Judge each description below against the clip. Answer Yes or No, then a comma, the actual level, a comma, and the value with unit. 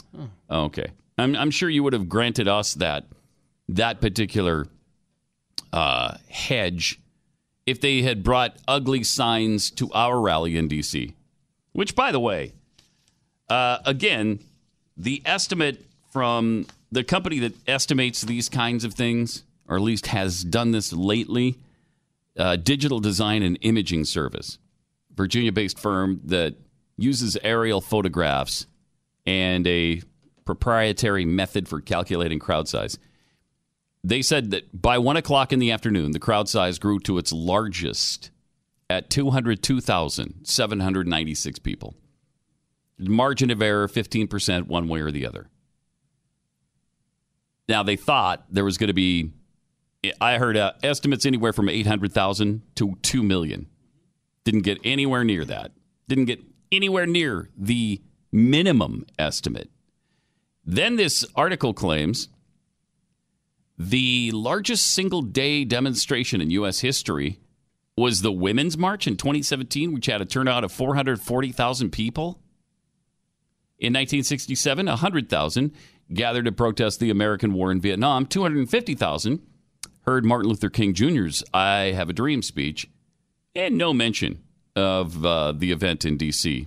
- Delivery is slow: Yes, slow, 125 wpm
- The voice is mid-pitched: No, low, 115 Hz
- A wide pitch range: Yes, wide, 5.7 semitones